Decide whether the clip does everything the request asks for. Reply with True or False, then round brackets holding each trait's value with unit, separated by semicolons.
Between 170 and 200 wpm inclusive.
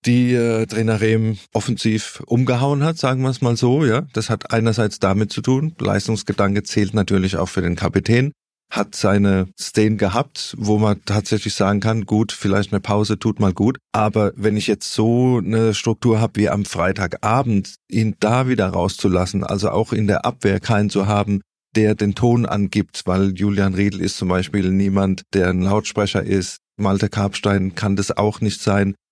True (180 wpm)